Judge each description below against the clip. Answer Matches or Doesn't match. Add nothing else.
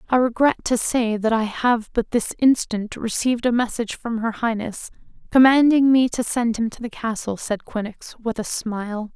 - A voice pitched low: Doesn't match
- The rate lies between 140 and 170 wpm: Doesn't match